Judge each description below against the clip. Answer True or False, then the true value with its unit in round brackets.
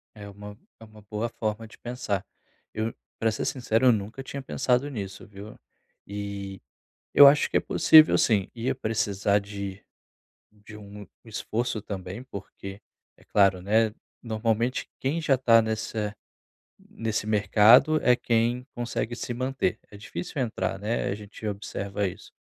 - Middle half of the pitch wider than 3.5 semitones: False (2.8 semitones)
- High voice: False (110 Hz)